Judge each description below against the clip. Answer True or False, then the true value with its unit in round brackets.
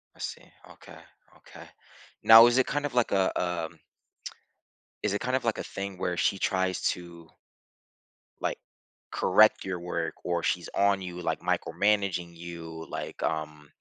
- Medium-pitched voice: False (90 Hz)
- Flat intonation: False (3.1 semitones)